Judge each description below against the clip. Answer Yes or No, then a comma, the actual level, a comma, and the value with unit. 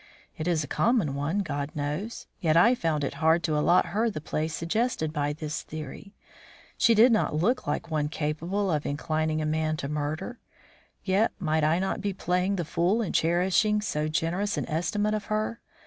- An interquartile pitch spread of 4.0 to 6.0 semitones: Yes, average, 5.0 semitones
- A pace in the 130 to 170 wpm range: No, average, 190 wpm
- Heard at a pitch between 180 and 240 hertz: No, medium, 165 Hz